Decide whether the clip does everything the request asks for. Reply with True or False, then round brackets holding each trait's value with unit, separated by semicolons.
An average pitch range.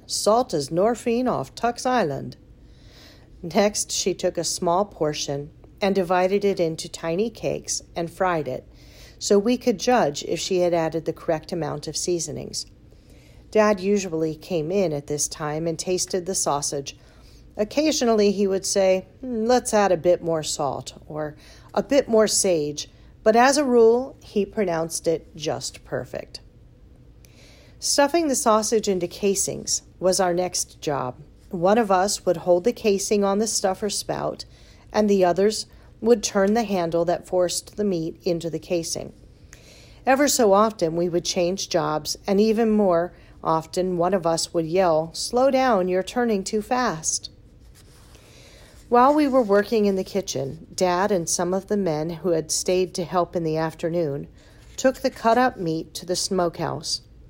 True (4.4 semitones)